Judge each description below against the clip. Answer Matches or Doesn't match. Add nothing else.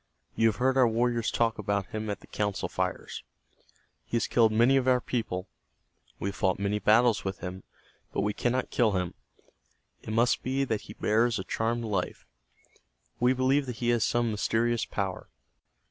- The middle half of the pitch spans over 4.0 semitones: Doesn't match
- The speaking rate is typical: Matches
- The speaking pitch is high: Doesn't match